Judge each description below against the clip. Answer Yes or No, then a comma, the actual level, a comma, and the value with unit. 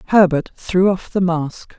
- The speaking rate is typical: Yes, average, 170 wpm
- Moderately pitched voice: Yes, medium, 180 Hz